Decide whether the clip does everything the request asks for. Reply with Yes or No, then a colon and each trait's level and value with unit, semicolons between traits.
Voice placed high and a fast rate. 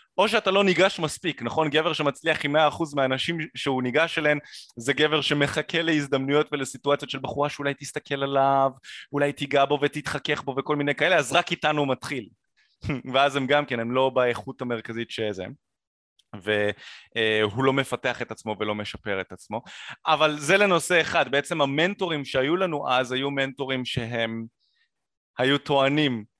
No: medium, 140 Hz; fast, 155 wpm